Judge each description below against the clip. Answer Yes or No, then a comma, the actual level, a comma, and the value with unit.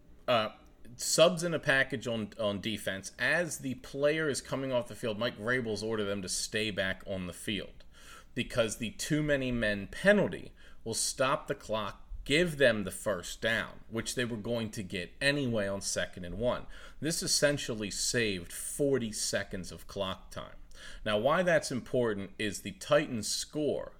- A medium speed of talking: Yes, average, 170 wpm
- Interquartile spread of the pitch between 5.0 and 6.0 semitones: Yes, average, 5.3 semitones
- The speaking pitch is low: Yes, low, 115 Hz